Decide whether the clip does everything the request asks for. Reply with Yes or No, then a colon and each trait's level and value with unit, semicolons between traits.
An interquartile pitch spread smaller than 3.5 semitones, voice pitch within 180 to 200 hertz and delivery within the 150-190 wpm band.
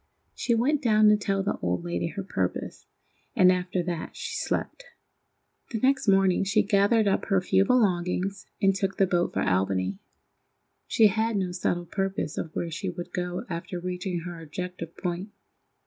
Yes: average, 2.8 semitones; medium, 185 Hz; average, 170 wpm